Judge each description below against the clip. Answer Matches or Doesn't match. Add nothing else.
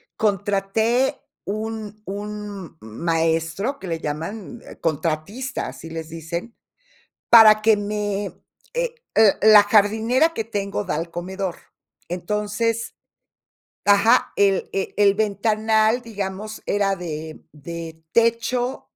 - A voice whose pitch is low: Doesn't match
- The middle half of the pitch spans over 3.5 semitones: Matches